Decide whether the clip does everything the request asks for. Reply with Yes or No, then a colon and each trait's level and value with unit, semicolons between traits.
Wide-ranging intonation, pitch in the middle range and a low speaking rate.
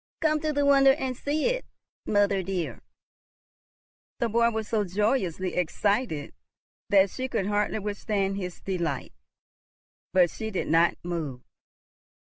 No: wide, 5.8 semitones; high, 205 Hz; slow, 130 wpm